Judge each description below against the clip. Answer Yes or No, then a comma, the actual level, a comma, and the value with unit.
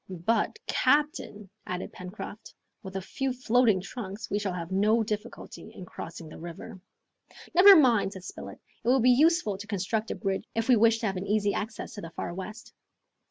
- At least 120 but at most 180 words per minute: No, average, 190 wpm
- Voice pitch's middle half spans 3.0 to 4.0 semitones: Yes, average, 3.6 semitones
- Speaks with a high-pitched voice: Yes, high, 210 Hz